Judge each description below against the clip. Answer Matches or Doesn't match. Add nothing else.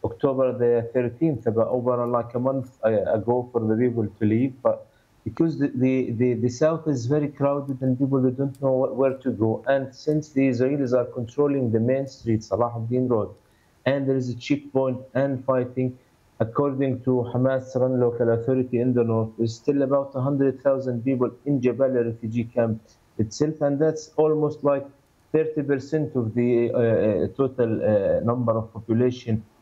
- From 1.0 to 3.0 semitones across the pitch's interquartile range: Matches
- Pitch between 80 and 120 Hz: Doesn't match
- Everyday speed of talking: Matches